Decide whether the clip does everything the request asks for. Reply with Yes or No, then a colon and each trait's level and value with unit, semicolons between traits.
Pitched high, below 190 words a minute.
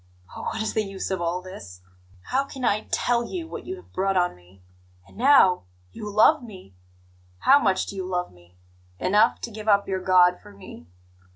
No: high, 195 Hz; average, 200 wpm